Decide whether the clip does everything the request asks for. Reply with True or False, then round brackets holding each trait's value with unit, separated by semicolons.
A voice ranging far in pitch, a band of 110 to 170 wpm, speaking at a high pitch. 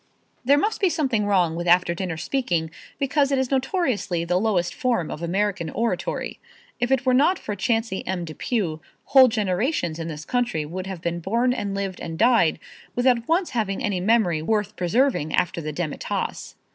False (6.6 semitones; 180 wpm; 205 Hz)